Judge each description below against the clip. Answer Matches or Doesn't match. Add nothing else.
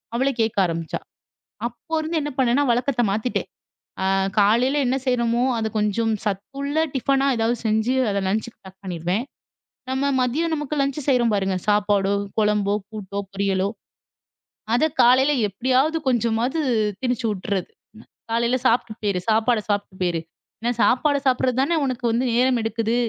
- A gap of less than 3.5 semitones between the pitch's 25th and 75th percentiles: Doesn't match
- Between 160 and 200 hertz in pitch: Doesn't match